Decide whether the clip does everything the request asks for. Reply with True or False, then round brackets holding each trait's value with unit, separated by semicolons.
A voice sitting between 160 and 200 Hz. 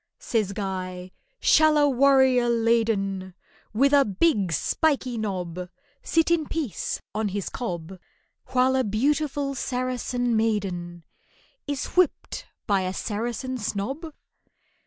False (230 Hz)